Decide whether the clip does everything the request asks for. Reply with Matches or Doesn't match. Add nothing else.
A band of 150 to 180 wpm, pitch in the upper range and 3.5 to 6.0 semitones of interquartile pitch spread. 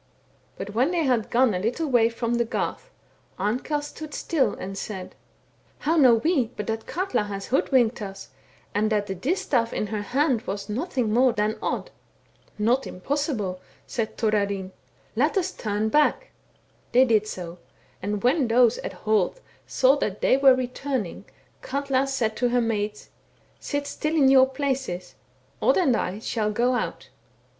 Matches